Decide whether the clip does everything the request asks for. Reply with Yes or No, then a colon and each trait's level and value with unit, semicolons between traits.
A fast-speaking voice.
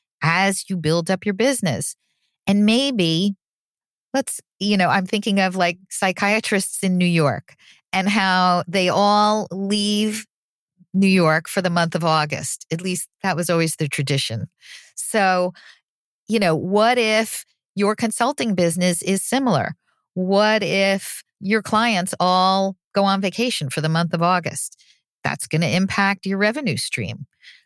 No: average, 150 wpm